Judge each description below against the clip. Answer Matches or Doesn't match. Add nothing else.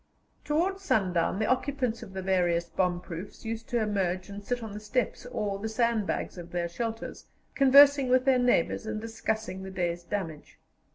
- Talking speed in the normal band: Matches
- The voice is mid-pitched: Doesn't match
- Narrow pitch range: Doesn't match